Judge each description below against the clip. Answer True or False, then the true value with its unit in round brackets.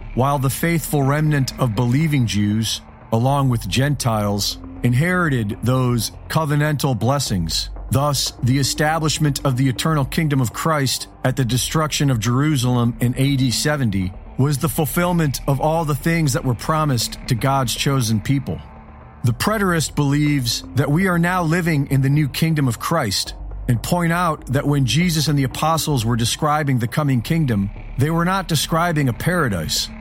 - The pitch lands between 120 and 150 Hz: True (135 Hz)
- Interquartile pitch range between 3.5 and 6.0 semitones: True (4.5 semitones)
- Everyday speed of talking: True (160 wpm)